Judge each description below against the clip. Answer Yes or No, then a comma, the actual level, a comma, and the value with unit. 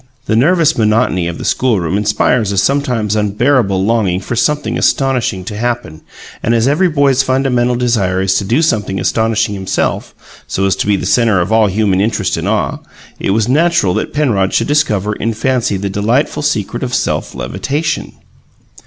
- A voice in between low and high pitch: No, low, 110 Hz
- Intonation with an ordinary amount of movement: Yes, average, 4.9 semitones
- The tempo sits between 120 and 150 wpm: No, average, 175 wpm